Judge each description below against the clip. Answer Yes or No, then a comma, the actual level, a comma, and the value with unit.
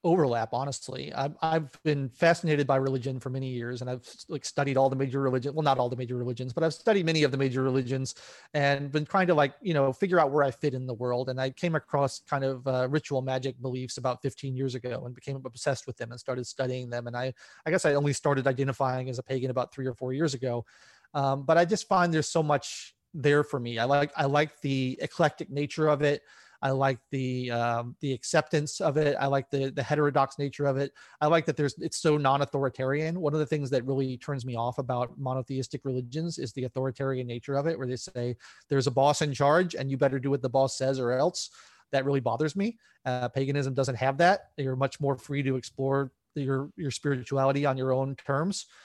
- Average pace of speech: No, fast, 230 wpm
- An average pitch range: No, narrow, 2.2 semitones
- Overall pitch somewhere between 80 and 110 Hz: No, low, 135 Hz